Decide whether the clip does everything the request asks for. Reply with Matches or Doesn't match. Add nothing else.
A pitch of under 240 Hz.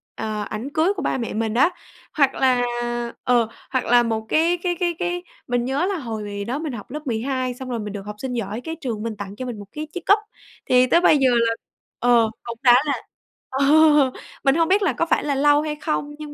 Doesn't match